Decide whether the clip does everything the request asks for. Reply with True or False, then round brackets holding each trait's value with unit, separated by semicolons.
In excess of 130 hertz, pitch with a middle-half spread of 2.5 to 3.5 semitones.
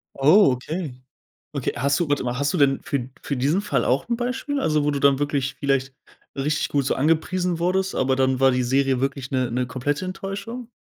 False (140 Hz; 5.0 semitones)